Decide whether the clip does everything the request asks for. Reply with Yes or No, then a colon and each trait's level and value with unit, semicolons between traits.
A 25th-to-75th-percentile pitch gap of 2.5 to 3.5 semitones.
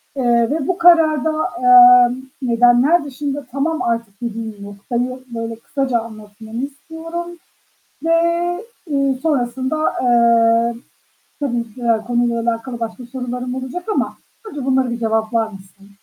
Yes: average, 3.1 semitones